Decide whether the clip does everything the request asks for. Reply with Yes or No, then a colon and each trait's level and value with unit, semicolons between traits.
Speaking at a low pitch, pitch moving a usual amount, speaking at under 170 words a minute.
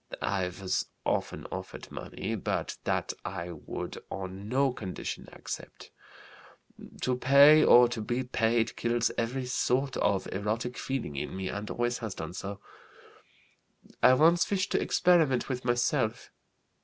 Yes: low, 120 Hz; average, 4.5 semitones; average, 140 wpm